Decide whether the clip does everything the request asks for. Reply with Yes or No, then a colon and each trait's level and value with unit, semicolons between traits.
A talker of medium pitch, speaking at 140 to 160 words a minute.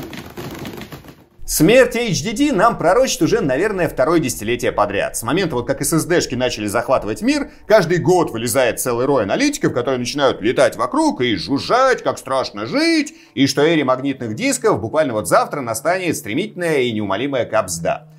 Yes: medium, 165 Hz; average, 150 wpm